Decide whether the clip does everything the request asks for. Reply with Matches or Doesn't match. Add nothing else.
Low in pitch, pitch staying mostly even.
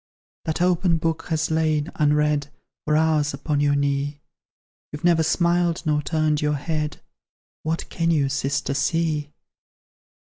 Doesn't match